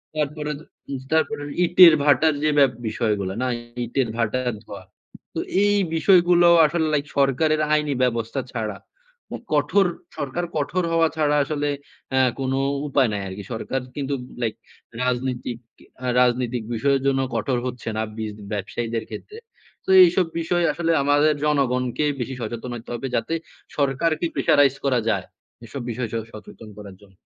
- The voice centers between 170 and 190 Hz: No, low, 135 Hz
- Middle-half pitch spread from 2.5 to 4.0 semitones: No, average, 4.5 semitones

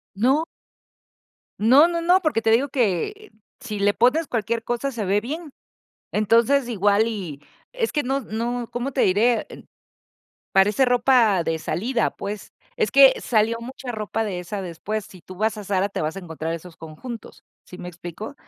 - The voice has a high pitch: Yes, high, 225 Hz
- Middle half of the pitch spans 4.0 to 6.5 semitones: Yes, average, 4.8 semitones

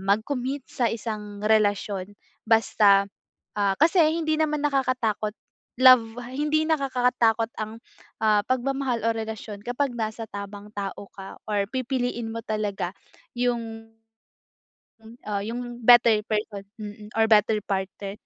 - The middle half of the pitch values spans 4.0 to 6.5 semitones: No, average, 3.2 semitones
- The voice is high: Yes, high, 225 Hz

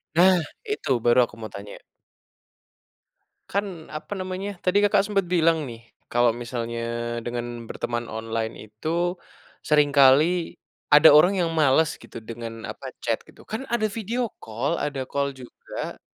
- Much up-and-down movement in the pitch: Yes, wide, 7.6 semitones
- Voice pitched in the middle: Yes, medium, 150 Hz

